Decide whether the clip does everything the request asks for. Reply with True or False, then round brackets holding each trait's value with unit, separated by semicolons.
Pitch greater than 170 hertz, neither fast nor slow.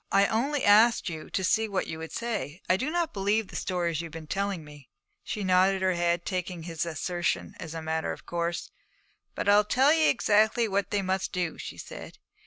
False (190 Hz; 210 wpm)